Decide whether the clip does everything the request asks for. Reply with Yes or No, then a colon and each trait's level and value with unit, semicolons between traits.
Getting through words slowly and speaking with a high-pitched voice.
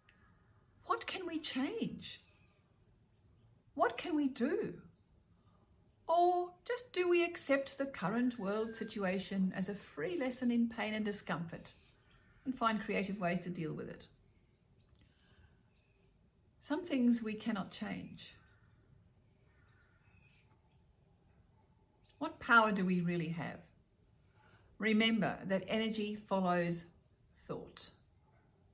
Yes: slow, 100 wpm; high, 200 Hz